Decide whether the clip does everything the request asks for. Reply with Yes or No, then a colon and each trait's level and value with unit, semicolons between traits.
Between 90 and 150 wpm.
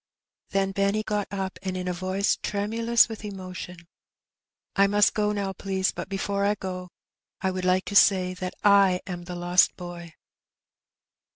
No: average, 170 wpm